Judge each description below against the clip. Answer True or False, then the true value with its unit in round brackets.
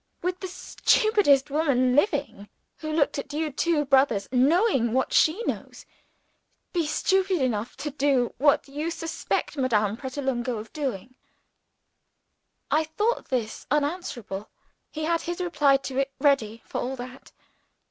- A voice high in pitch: True (280 Hz)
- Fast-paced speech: False (135 wpm)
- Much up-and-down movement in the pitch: False (4.0 semitones)